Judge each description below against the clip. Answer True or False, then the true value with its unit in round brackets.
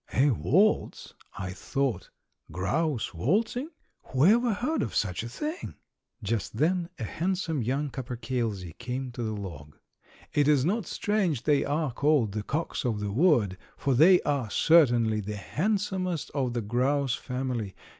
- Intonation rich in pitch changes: True (6.9 semitones)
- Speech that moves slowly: False (145 wpm)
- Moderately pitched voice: False (130 Hz)